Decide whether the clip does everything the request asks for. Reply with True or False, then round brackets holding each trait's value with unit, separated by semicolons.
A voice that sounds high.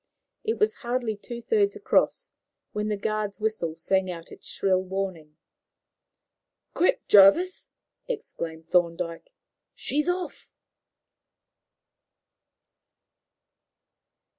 True (210 Hz)